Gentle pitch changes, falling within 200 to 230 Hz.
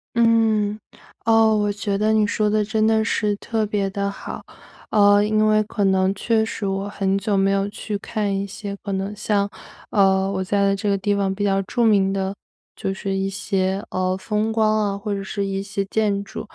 Yes: narrow, 1.6 semitones; high, 205 Hz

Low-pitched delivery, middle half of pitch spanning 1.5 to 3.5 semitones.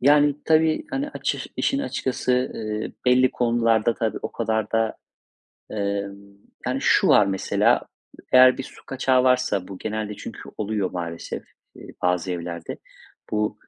No: low, 110 Hz; average, 4.2 semitones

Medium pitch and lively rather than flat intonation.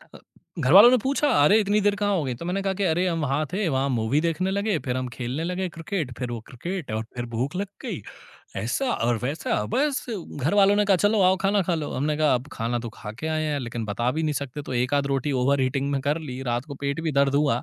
Yes: medium, 150 Hz; wide, 6.6 semitones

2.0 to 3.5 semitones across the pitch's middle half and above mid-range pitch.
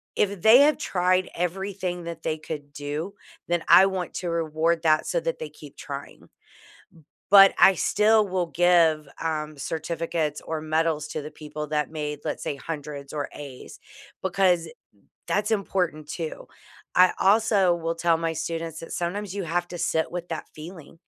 No: average, 3.2 semitones; medium, 165 Hz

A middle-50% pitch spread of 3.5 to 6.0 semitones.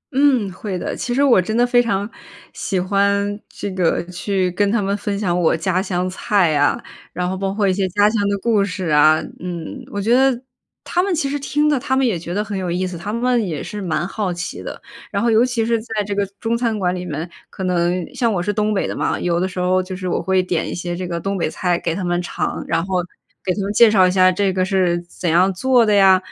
No: average, 3.1 semitones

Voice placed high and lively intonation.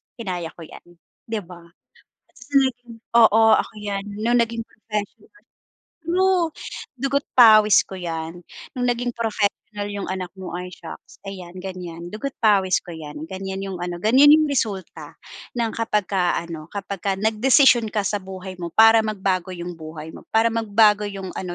No: high, 200 Hz; average, 4.1 semitones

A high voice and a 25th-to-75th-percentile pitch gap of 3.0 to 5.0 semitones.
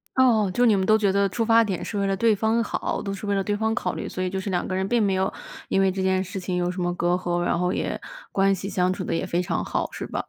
No: high, 195 Hz; narrow, 2.5 semitones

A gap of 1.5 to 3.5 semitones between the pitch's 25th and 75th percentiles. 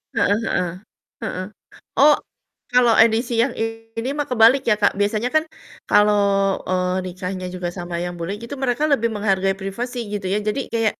No: average, 4.0 semitones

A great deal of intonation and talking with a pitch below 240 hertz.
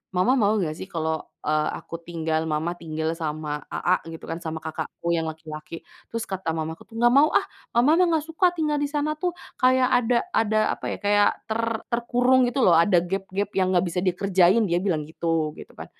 Yes: wide, 6.9 semitones; medium, 185 Hz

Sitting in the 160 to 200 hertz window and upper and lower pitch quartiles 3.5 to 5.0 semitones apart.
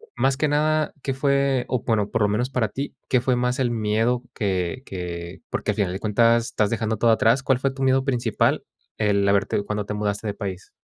No: low, 115 Hz; average, 4.2 semitones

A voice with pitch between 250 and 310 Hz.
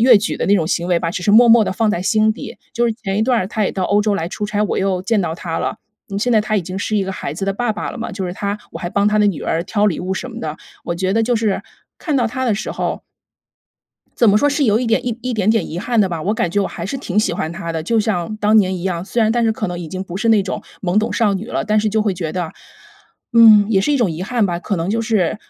No: high, 205 Hz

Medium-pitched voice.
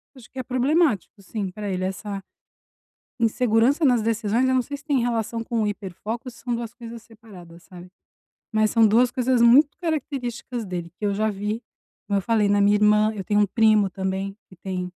No: high, 220 Hz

